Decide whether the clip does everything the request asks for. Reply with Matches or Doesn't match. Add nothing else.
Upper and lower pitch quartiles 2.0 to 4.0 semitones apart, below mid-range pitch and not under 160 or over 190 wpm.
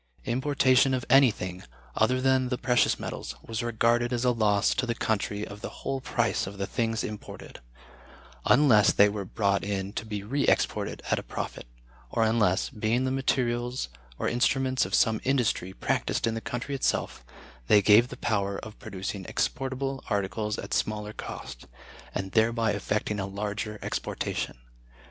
Matches